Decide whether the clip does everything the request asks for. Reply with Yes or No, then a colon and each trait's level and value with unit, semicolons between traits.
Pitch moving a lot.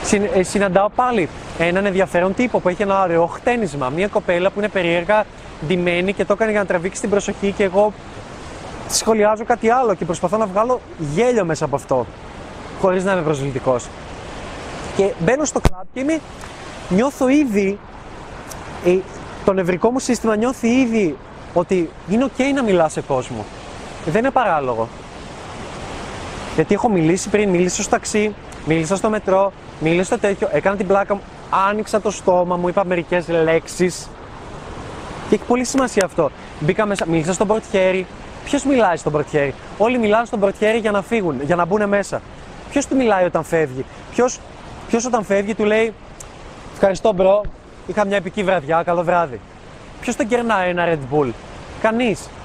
No: average, 4.0 semitones